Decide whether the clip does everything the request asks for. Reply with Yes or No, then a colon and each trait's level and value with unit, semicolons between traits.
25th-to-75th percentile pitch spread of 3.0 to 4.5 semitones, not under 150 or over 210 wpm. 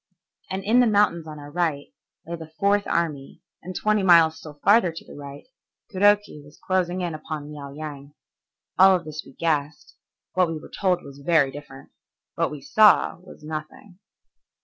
Yes: average, 4.1 semitones; average, 175 wpm